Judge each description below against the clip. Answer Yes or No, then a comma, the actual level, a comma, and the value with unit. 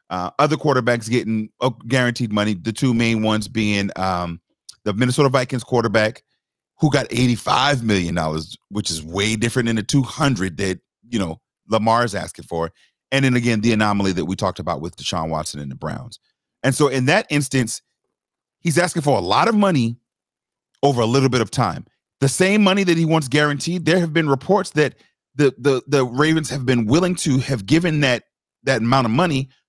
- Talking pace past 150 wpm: Yes, average, 195 wpm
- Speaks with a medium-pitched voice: No, low, 125 Hz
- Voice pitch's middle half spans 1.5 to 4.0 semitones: No, average, 5.2 semitones